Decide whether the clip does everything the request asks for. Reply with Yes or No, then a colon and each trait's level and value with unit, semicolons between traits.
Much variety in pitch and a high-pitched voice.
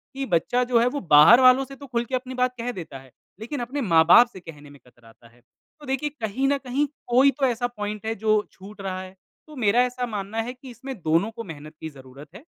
Yes: wide, 6.0 semitones; high, 230 Hz